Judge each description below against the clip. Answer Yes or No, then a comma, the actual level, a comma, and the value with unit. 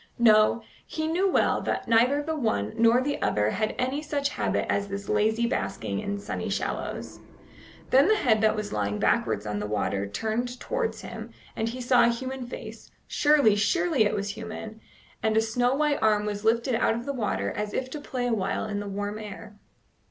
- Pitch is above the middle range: Yes, high, 225 Hz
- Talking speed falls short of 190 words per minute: No, average, 195 wpm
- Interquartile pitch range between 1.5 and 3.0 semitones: No, average, 4.1 semitones